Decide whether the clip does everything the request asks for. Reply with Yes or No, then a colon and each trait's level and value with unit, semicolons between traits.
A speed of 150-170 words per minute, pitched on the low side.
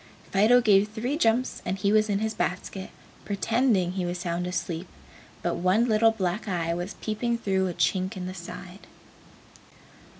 No: average, 165 wpm; high, 195 Hz